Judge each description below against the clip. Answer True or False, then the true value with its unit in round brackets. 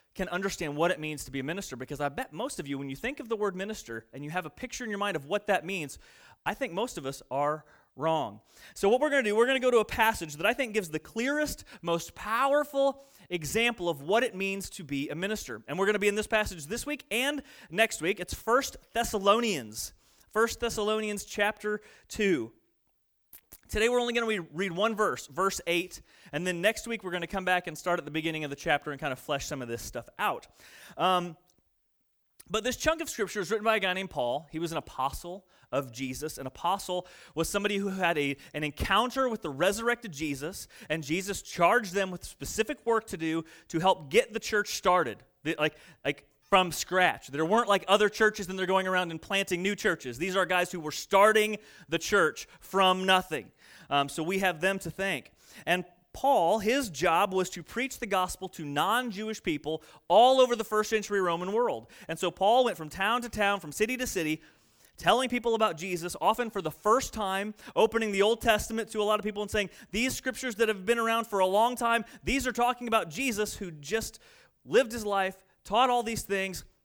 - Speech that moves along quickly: True (225 wpm)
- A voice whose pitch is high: True (195 Hz)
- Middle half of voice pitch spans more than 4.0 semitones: True (5.1 semitones)